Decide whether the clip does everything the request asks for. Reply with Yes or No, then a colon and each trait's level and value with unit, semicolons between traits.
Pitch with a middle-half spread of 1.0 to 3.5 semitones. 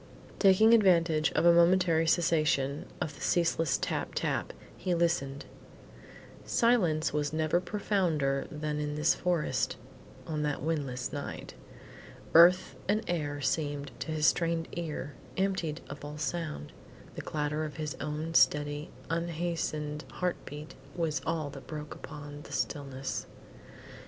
Yes: narrow, 2.6 semitones